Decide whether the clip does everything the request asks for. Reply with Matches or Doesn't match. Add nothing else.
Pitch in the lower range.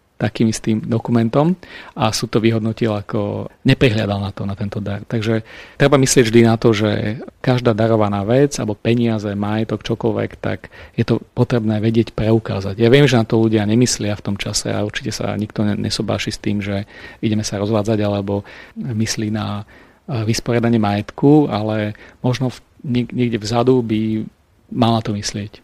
Matches